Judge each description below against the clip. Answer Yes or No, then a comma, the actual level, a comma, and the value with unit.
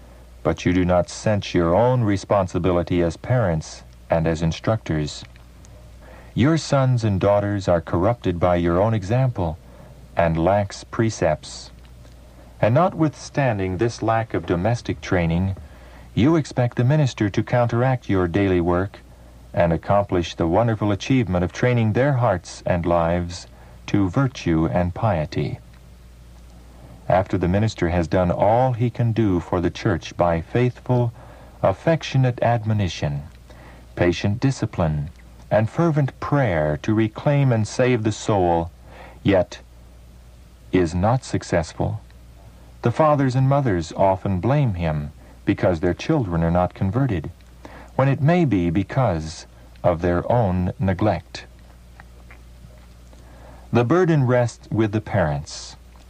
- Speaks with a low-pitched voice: Yes, very low, 90 Hz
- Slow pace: Yes, slow, 125 wpm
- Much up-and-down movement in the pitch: Yes, wide, 7.8 semitones